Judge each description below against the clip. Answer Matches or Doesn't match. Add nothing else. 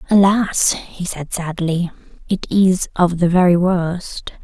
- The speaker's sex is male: Doesn't match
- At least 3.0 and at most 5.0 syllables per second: Matches